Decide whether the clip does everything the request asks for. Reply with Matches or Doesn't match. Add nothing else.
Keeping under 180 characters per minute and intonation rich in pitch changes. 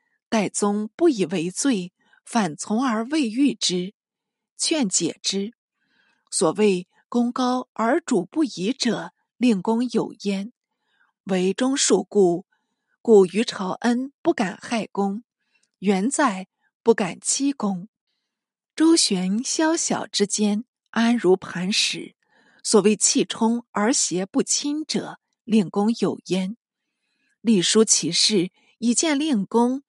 Doesn't match